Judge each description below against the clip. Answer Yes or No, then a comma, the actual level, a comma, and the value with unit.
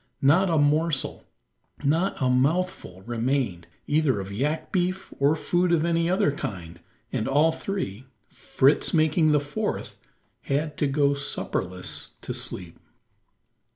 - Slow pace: Yes, slow, 130 wpm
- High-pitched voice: No, medium, 145 Hz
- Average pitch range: Yes, average, 4.5 semitones